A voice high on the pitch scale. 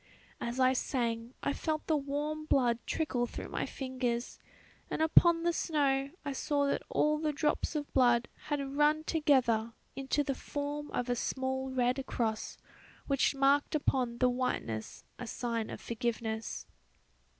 Yes: very high, 270 Hz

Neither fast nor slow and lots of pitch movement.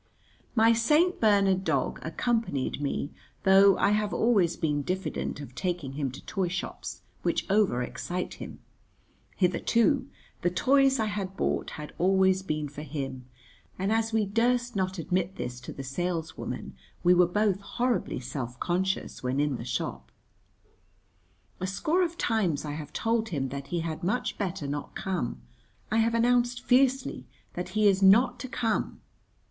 Yes: average, 160 wpm; wide, 6.8 semitones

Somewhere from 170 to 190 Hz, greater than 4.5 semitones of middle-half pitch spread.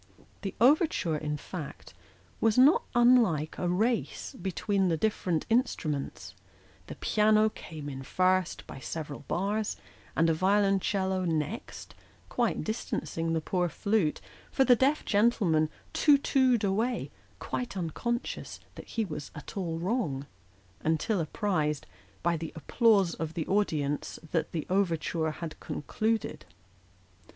Yes: medium, 185 Hz; wide, 5.5 semitones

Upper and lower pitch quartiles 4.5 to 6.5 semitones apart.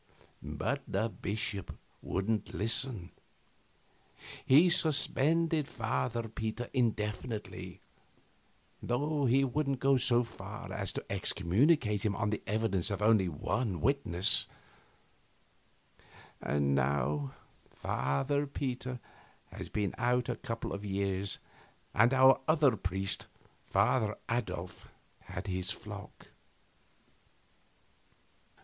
Yes: average, 5.0 semitones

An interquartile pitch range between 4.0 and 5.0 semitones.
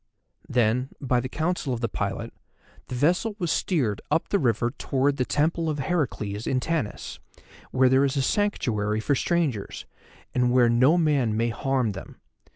Yes: average, 4.7 semitones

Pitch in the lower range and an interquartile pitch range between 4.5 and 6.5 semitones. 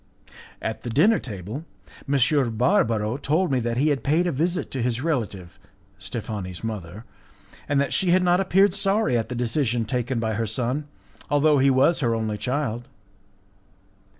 Yes: low, 125 Hz; average, 5.2 semitones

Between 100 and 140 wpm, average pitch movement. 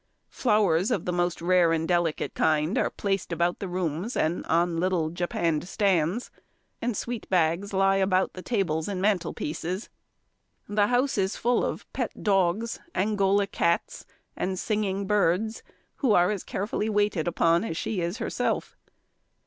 No: average, 150 wpm; average, 3.3 semitones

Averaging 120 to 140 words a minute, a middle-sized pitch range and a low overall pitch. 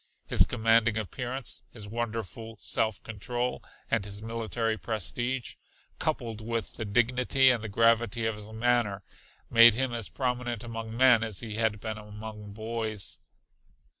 No: slow, 135 wpm; narrow, 1.7 semitones; low, 115 Hz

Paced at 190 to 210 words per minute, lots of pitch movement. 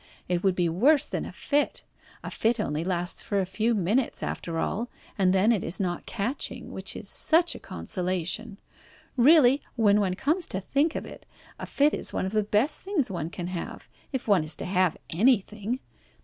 Yes: average, 195 wpm; wide, 5.9 semitones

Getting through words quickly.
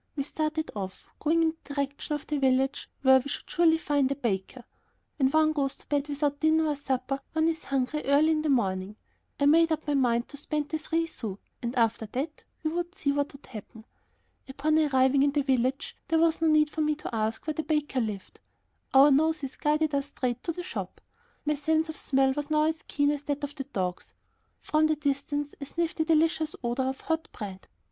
Yes: fast, 215 wpm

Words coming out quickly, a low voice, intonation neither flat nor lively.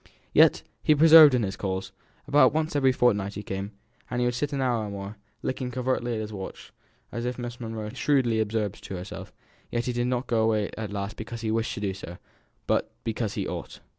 Yes: fast, 215 wpm; low, 115 Hz; average, 3.4 semitones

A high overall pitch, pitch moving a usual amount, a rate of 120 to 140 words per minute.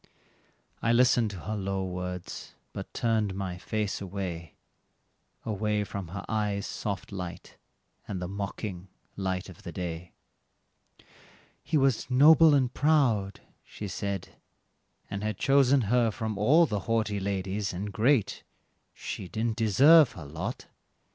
No: low, 105 Hz; average, 3.5 semitones; slow, 135 wpm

